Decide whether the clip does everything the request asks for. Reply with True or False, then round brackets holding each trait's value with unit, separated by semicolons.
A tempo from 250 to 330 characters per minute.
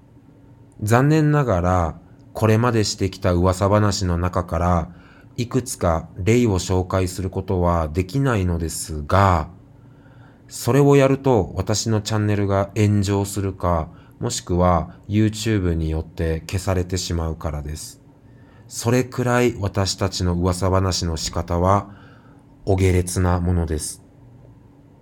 True (260 characters per minute)